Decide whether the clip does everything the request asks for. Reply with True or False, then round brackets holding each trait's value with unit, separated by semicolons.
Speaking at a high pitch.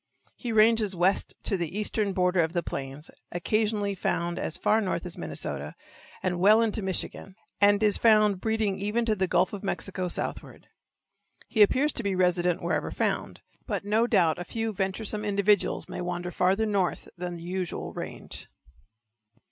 True (195 Hz)